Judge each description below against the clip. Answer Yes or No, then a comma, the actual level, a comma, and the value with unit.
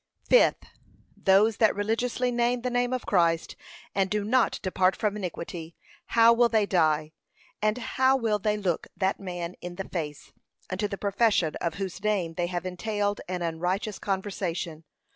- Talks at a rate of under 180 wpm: Yes, average, 160 wpm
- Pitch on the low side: No, high, 200 Hz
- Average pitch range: Yes, average, 3.8 semitones